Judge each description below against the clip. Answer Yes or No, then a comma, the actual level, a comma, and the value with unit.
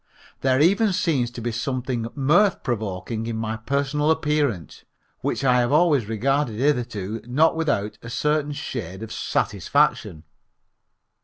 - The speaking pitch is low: Yes, low, 130 Hz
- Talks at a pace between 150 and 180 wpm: No, slow, 135 wpm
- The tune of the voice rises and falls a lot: No, average, 4.9 semitones